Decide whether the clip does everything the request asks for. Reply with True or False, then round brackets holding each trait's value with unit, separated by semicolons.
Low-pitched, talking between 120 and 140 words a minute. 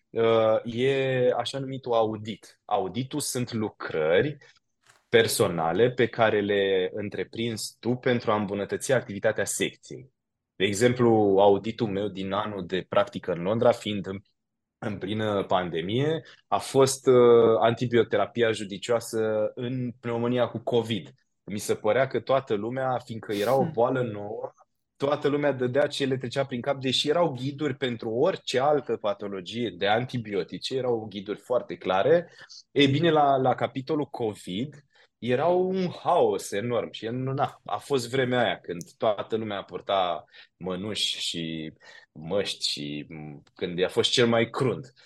True (120 Hz; 135 wpm)